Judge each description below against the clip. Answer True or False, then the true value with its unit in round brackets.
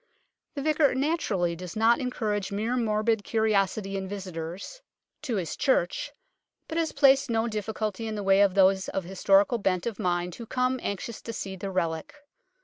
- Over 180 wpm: True (190 wpm)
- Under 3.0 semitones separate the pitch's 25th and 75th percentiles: False (3.8 semitones)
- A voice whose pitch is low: False (210 Hz)